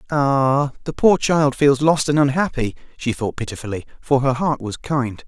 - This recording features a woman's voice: No, male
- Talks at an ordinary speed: Yes, average, 180 wpm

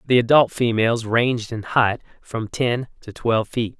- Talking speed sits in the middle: Yes, average, 175 wpm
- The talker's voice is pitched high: No, low, 115 Hz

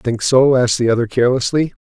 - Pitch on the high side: No, low, 125 Hz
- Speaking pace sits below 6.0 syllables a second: No, 6.4 syllables/s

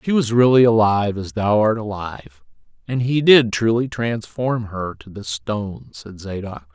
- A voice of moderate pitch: No, low, 110 Hz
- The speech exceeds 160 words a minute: Yes, average, 170 wpm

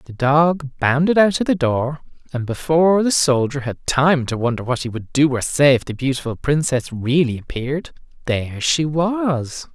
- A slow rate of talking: No, average, 185 wpm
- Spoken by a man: Yes, male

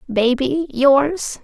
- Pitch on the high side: Yes, very high, 275 Hz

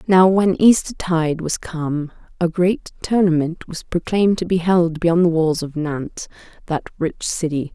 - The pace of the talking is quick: No, average, 165 wpm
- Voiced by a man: No, female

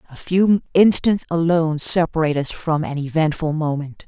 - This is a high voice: No, medium, 160 Hz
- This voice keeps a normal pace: Yes, average, 145 wpm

